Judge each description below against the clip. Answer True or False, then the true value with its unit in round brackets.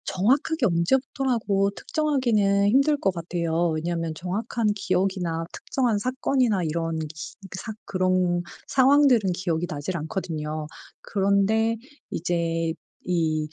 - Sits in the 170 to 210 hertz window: True (190 Hz)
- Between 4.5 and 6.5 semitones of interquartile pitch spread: True (5.3 semitones)